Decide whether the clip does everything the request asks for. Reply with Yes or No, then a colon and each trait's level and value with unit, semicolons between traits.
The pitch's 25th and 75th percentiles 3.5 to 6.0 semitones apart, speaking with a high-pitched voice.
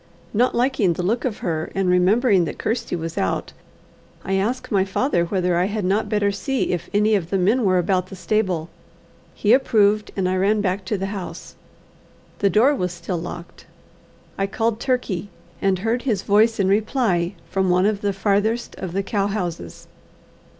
No: average, 3.1 semitones; high, 195 Hz